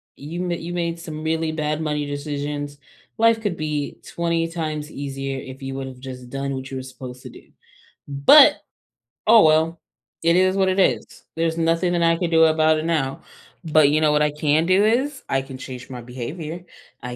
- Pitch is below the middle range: No, medium, 155 Hz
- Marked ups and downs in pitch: No, average, 3.5 semitones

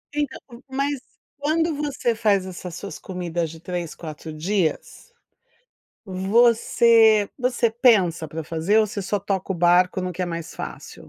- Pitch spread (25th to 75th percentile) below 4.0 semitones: No, average, 5.1 semitones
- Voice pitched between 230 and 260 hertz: No, high, 195 Hz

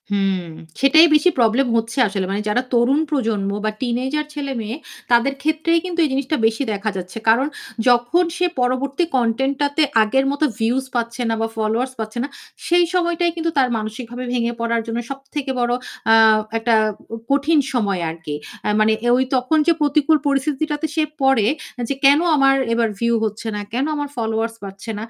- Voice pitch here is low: No, very high, 250 Hz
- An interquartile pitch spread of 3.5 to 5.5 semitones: Yes, average, 4.2 semitones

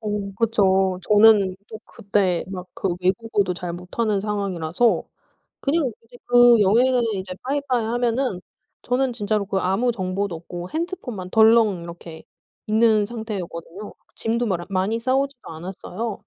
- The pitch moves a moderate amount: Yes, average, 4.1 semitones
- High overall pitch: Yes, high, 210 Hz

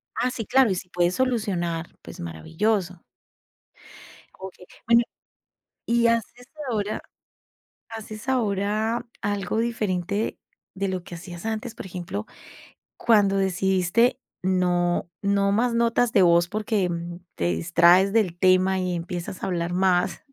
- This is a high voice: Yes, high, 195 Hz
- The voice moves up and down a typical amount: Yes, average, 3.9 semitones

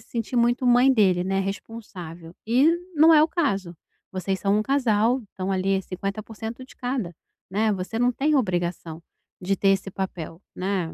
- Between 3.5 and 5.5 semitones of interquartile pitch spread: Yes, average, 4.6 semitones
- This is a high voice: Yes, high, 200 Hz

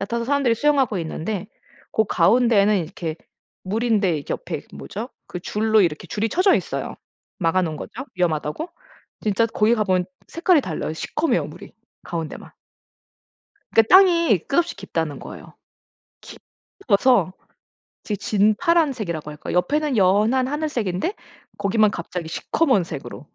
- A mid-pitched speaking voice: No, high, 210 Hz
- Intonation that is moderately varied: No, wide, 6.6 semitones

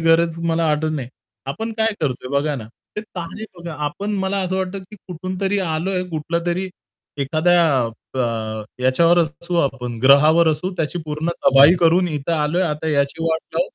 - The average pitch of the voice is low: No, medium, 165 Hz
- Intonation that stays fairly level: No, average, 3.3 semitones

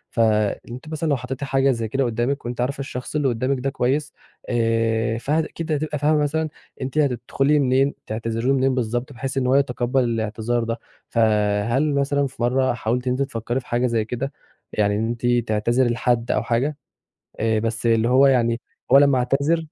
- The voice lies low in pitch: Yes, low, 125 Hz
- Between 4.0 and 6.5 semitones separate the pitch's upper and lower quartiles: No, average, 3.0 semitones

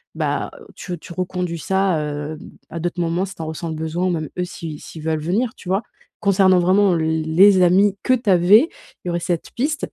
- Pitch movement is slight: No, average, 3.1 semitones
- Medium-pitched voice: Yes, medium, 180 Hz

